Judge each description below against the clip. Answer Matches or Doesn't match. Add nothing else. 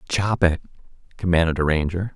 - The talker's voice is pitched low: Matches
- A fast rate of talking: Doesn't match